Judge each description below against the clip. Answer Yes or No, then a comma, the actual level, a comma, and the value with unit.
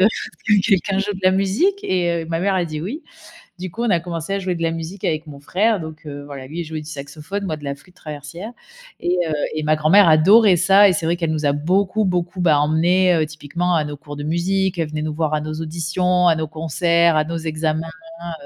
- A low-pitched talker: No, medium, 165 Hz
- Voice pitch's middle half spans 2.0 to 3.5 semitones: Yes, average, 3.1 semitones